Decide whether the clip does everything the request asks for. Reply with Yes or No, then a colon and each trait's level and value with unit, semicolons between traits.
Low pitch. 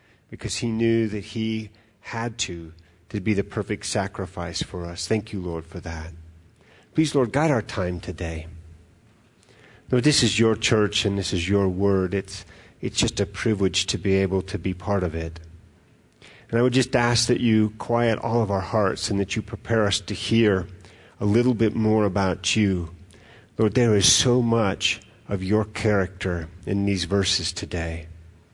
Yes: low, 100 Hz